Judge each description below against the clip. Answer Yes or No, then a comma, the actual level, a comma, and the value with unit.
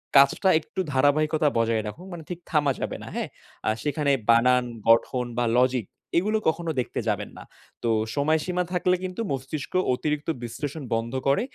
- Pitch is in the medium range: Yes, medium, 145 Hz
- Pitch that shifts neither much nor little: Yes, average, 4.4 semitones